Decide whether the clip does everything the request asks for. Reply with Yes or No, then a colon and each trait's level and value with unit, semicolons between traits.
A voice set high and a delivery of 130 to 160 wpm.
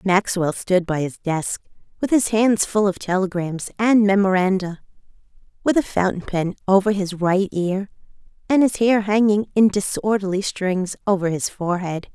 Yes: high, 195 Hz; average, 155 wpm